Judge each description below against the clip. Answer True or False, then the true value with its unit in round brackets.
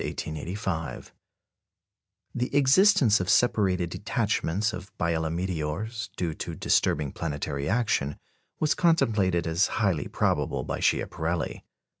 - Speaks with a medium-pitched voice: False (90 Hz)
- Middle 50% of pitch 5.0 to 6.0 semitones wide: True (5.4 semitones)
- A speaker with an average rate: False (105 wpm)